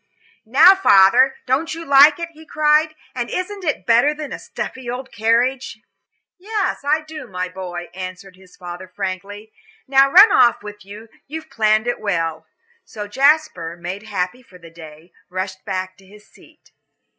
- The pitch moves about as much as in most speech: No, wide, 7.9 semitones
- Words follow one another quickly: No, average, 165 wpm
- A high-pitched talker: Yes, high, 220 Hz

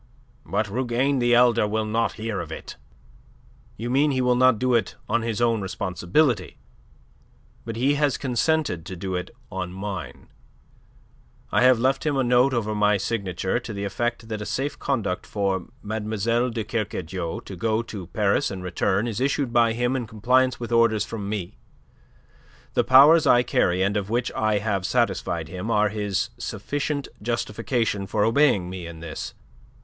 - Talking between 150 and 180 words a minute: Yes, average, 170 wpm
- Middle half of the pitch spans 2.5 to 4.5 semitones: Yes, average, 3.7 semitones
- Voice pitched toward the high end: No, low, 110 Hz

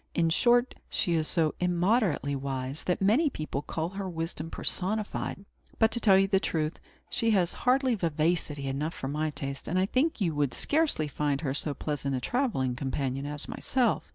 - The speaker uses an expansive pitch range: Yes, wide, 6.1 semitones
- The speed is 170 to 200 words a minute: Yes, average, 180 wpm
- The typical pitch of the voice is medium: Yes, medium, 165 Hz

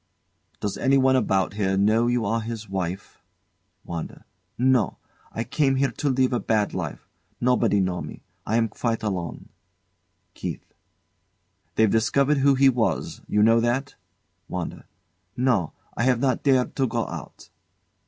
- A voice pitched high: No, low, 115 Hz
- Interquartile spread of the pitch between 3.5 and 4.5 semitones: Yes, average, 3.9 semitones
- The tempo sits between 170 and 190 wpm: No, average, 145 wpm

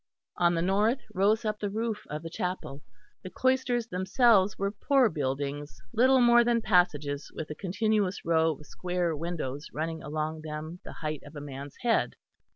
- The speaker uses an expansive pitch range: Yes, wide, 6.0 semitones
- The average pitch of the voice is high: No, medium, 180 Hz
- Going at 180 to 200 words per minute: No, average, 170 wpm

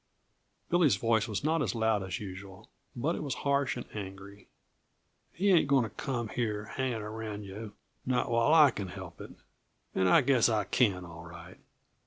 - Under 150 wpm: No, average, 180 wpm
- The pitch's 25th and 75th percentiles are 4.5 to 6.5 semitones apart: Yes, average, 4.8 semitones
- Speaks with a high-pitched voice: No, low, 110 Hz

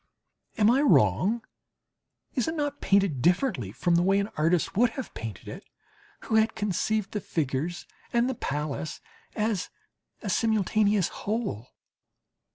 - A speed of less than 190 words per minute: Yes, average, 140 wpm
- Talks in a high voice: Yes, high, 200 Hz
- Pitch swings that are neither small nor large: No, wide, 5.8 semitones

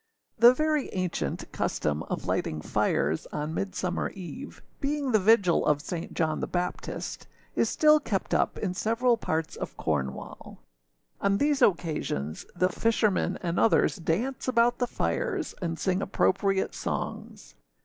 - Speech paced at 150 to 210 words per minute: No, average, 140 wpm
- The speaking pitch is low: No, high, 190 Hz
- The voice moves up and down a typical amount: No, wide, 6.8 semitones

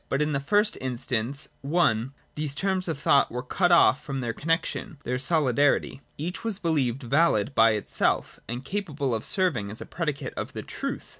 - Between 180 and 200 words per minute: Yes, average, 190 wpm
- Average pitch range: Yes, average, 5.0 semitones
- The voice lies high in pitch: No, medium, 140 Hz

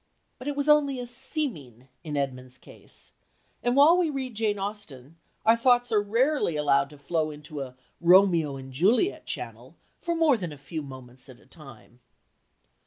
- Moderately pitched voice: Yes, medium, 175 Hz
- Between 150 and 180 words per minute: Yes, average, 175 wpm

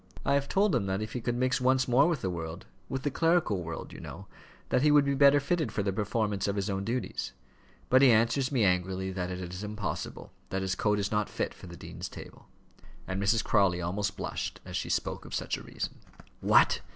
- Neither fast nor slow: No, fast, 230 wpm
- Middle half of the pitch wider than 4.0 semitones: Yes, wide, 5.5 semitones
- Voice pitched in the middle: No, low, 105 Hz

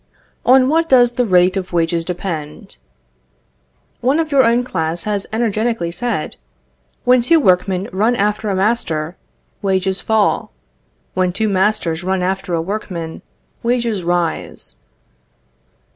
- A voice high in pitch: Yes, high, 195 Hz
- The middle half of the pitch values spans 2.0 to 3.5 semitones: No, average, 4.9 semitones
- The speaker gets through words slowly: Yes, slow, 130 wpm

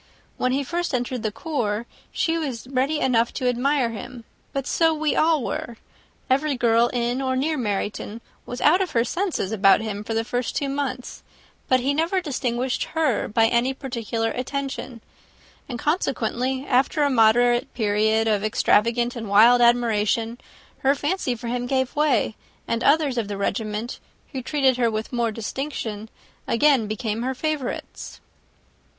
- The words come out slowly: No, average, 160 wpm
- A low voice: No, high, 245 Hz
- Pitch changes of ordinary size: Yes, average, 3.4 semitones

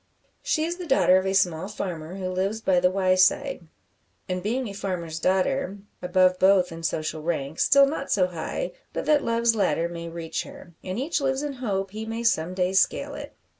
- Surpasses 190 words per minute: Yes, average, 200 wpm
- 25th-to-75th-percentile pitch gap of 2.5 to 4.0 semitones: No, average, 4.7 semitones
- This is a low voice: No, high, 190 Hz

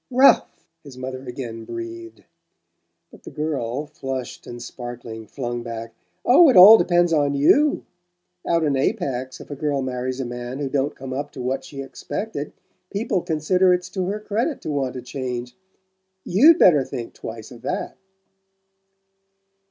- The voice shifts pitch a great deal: Yes, wide, 6.2 semitones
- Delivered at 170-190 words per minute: No, average, 160 wpm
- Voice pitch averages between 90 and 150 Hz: Yes, medium, 140 Hz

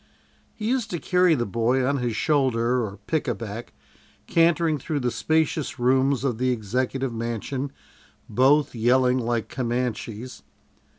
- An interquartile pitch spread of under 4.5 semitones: Yes, average, 3.3 semitones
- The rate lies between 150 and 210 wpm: No, average, 140 wpm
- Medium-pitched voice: No, low, 130 Hz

